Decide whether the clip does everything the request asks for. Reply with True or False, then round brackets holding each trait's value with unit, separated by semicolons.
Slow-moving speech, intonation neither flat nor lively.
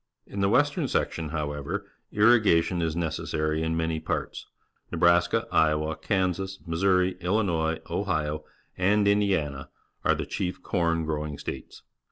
True (130 wpm; 3.5 semitones)